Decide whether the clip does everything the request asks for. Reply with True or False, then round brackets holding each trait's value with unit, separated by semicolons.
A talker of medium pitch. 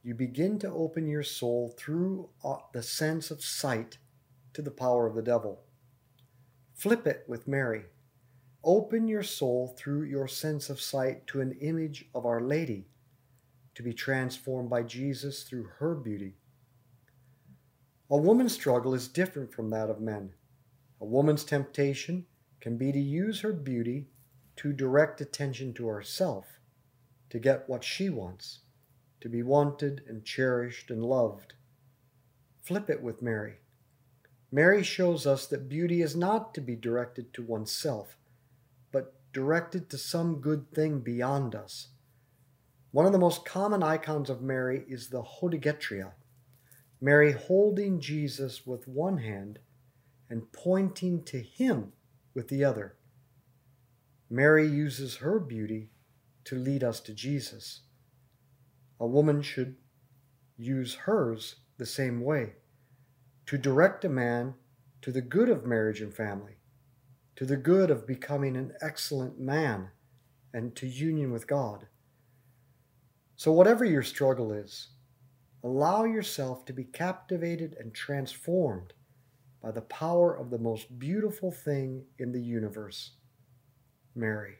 False (130 Hz)